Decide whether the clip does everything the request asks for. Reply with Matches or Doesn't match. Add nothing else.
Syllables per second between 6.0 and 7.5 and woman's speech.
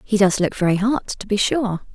Doesn't match